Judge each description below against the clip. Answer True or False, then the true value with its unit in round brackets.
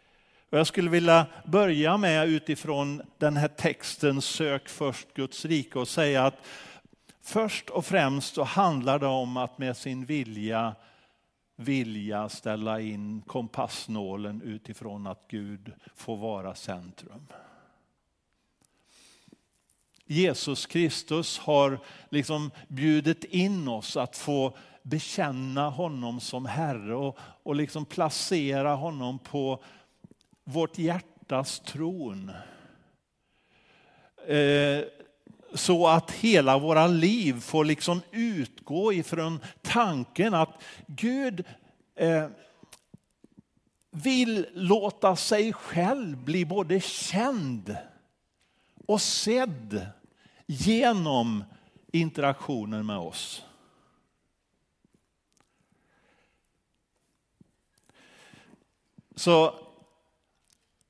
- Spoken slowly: True (85 wpm)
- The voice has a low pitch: False (150 Hz)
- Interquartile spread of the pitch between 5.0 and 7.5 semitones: True (5.3 semitones)